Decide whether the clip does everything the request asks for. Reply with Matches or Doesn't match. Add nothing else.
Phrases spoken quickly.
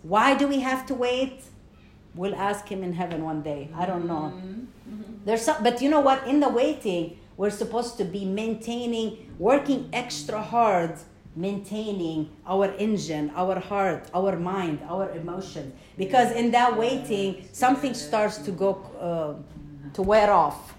Doesn't match